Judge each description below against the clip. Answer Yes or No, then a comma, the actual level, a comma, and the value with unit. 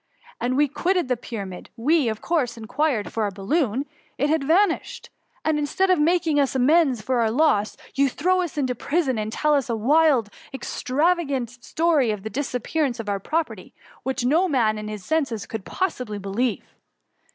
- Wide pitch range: Yes, wide, 5.8 semitones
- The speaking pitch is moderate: No, very high, 265 Hz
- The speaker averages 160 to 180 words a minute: No, average, 190 wpm